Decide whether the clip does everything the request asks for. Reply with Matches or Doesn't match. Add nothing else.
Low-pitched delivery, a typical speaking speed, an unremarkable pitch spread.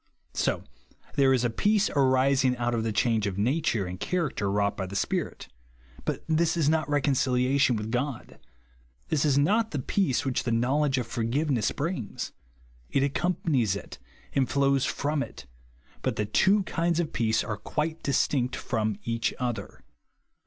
Matches